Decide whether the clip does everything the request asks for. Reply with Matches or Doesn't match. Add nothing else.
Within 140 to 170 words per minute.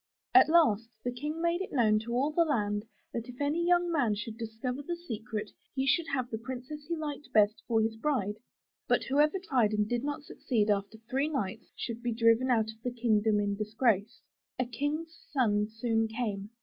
Doesn't match